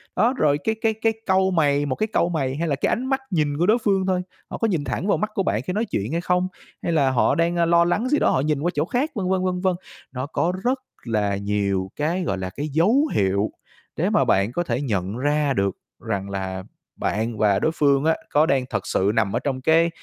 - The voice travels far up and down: Yes, wide, 8.1 semitones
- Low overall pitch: No, medium, 150 Hz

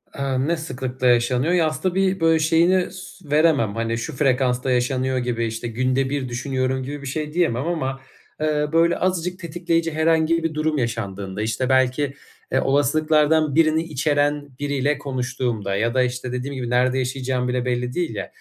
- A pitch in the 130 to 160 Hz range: Yes, low, 135 Hz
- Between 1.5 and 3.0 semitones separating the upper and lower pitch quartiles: No, average, 4.0 semitones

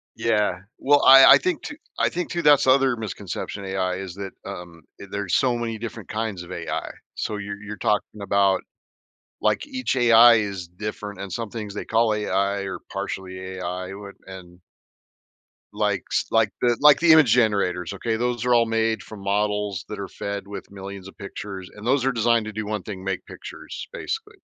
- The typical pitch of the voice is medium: No, low, 105 Hz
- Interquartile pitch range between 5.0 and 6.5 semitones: No, average, 3.2 semitones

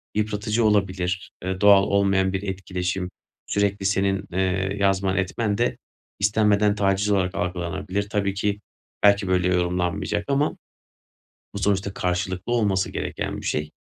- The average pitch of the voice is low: Yes, very low, 95 Hz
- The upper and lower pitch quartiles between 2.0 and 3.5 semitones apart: No, narrow, 1.6 semitones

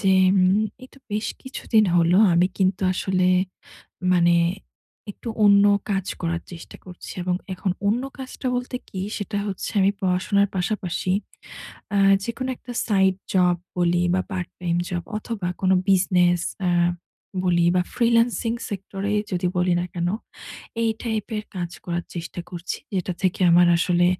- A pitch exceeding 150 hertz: Yes, medium, 185 Hz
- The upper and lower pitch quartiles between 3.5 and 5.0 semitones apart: No, narrow, 2.6 semitones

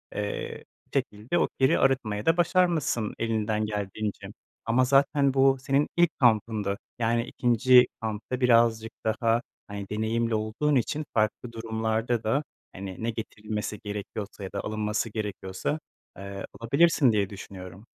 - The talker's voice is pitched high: No, low, 110 Hz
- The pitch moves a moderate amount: Yes, average, 3.3 semitones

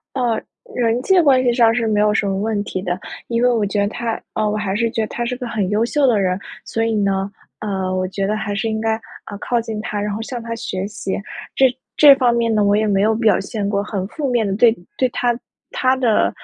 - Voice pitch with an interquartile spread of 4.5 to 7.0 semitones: No, average, 2.7 semitones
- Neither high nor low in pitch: No, high, 220 Hz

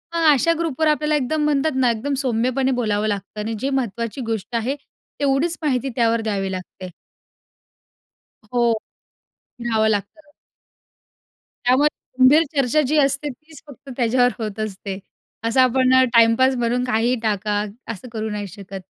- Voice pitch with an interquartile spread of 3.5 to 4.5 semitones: Yes, average, 4.0 semitones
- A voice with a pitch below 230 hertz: No, high, 245 Hz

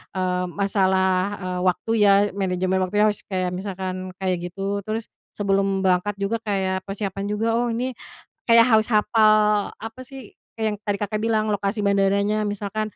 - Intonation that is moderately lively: No, narrow, 2.3 semitones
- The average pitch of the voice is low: No, high, 200 Hz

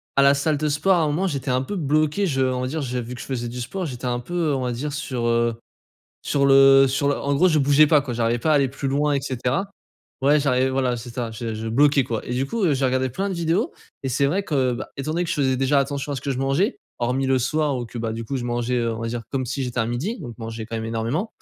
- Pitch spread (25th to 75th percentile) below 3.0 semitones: No, average, 3.3 semitones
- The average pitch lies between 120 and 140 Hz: Yes, low, 135 Hz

